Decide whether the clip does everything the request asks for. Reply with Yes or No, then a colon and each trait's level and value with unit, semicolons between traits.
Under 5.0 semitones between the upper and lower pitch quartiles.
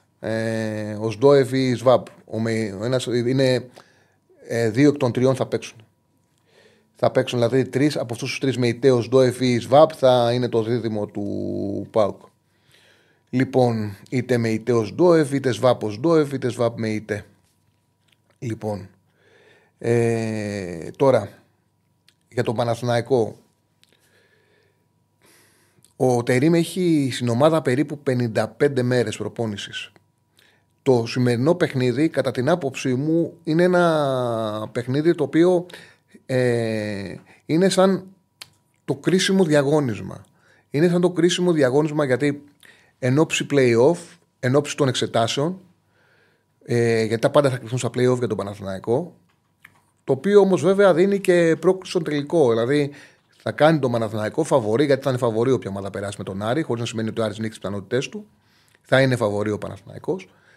Yes: average, 4.5 semitones